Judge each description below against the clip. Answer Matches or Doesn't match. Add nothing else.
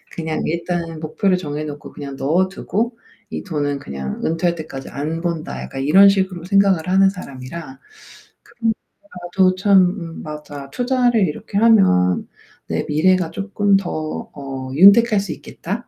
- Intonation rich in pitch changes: Doesn't match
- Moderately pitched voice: Matches